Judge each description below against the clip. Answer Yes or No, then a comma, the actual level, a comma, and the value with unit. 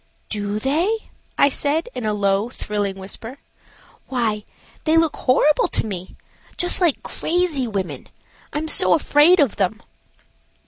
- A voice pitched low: No, very high, 255 Hz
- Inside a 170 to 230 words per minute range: No, average, 140 wpm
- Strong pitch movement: Yes, wide, 7.1 semitones